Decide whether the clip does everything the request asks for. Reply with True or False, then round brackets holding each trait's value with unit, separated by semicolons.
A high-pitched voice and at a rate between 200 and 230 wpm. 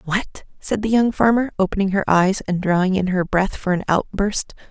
True (195 Hz; 205 wpm)